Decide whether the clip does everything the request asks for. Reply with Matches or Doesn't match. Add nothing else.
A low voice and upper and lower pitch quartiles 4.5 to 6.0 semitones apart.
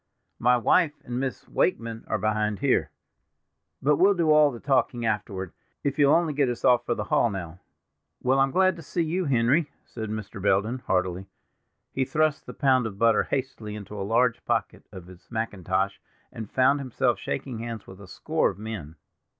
Matches